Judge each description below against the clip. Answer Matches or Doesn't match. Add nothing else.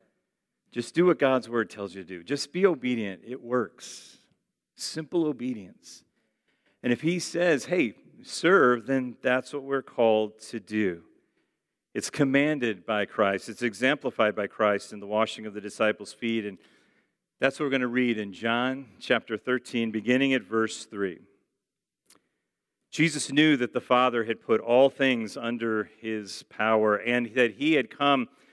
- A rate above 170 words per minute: Doesn't match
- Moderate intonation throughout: Matches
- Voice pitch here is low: Matches